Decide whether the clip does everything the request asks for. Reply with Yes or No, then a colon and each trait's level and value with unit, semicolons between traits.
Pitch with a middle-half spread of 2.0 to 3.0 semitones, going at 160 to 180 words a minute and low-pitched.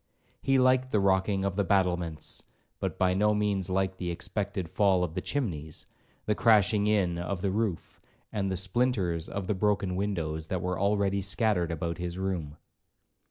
Yes: average, 2.7 semitones; average, 170 wpm; very low, 95 Hz